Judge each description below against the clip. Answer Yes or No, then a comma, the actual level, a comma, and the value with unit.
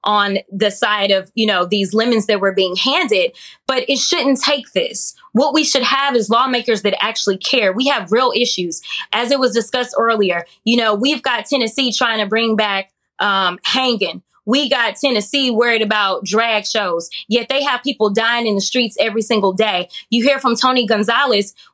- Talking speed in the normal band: Yes, average, 190 wpm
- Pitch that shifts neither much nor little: Yes, average, 4.3 semitones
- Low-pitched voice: No, high, 230 Hz